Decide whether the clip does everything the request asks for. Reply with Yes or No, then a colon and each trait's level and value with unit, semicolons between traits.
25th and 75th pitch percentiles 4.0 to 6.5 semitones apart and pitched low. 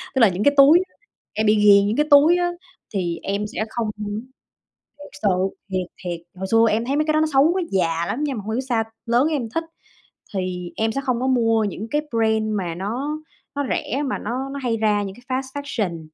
No: average, 5.1 semitones; high, 225 Hz